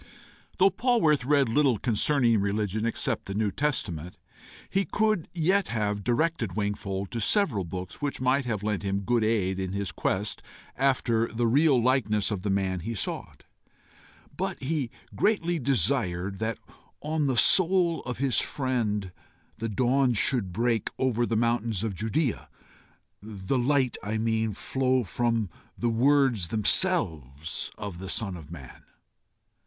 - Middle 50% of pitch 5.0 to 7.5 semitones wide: Yes, average, 5.3 semitones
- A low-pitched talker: Yes, low, 115 Hz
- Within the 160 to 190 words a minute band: No, average, 145 wpm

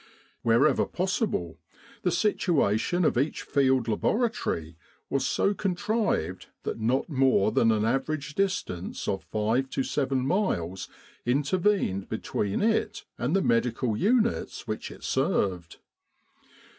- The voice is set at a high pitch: No, low, 135 Hz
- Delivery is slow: Yes, slow, 120 wpm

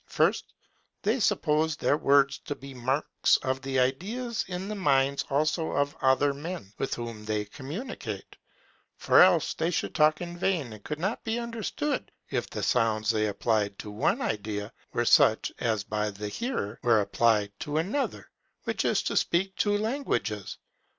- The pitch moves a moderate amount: No, wide, 8.5 semitones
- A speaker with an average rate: Yes, average, 165 wpm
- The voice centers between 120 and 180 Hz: Yes, medium, 140 Hz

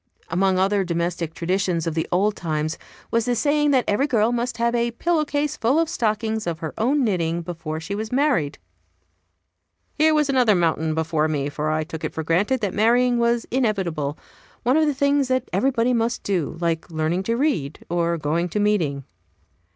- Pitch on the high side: Yes, high, 205 Hz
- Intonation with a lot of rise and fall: Yes, wide, 6.9 semitones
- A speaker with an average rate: Yes, average, 190 wpm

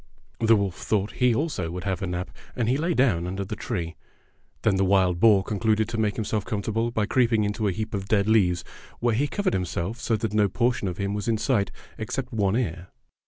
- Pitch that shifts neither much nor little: Yes, average, 3.0 semitones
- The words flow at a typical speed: No, fast, 220 wpm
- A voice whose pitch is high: No, low, 105 Hz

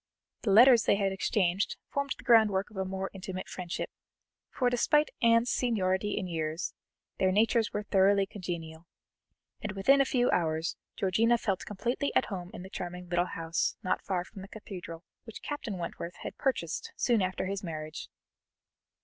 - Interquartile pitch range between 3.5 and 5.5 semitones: Yes, average, 4.1 semitones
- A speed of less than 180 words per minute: Yes, average, 165 wpm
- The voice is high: Yes, high, 195 Hz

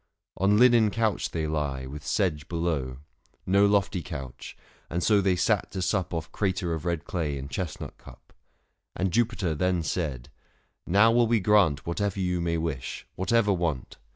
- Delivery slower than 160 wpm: No, average, 175 wpm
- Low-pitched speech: Yes, very low, 90 Hz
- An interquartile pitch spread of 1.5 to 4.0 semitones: No, average, 4.5 semitones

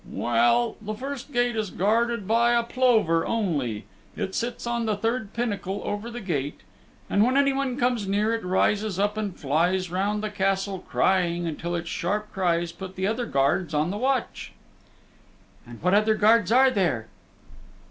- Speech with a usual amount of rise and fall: Yes, average, 4.6 semitones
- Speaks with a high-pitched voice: Yes, high, 205 Hz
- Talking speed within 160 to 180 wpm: Yes, average, 170 wpm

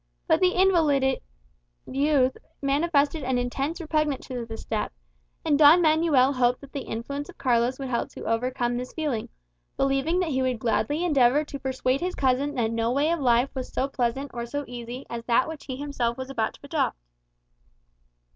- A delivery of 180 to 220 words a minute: Yes, average, 185 wpm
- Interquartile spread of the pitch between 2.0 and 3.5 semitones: Yes, average, 3.1 semitones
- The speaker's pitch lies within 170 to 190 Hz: No, very high, 270 Hz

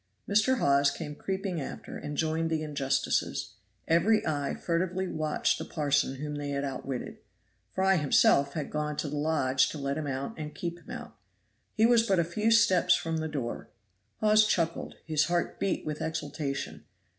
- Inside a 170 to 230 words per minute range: Yes, average, 175 wpm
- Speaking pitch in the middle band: Yes, medium, 155 Hz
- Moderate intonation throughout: Yes, average, 3.9 semitones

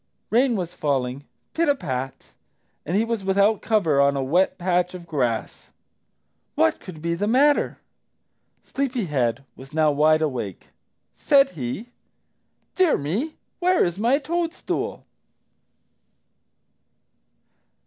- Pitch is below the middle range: No, medium, 180 Hz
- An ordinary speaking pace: No, slow, 120 wpm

